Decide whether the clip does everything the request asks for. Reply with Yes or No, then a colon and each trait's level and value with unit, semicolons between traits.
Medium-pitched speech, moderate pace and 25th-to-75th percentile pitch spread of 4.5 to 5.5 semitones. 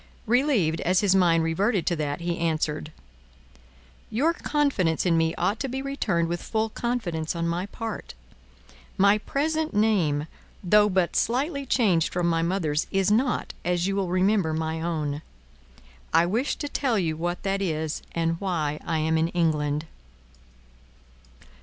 Yes: medium, 175 Hz; average, 155 wpm; average, 4.9 semitones